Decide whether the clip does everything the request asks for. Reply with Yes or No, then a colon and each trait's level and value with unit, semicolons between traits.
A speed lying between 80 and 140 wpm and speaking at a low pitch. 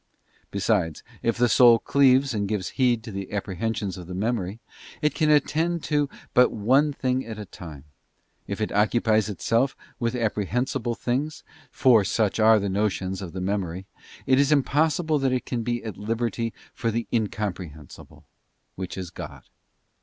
No: average, 155 wpm; low, 115 Hz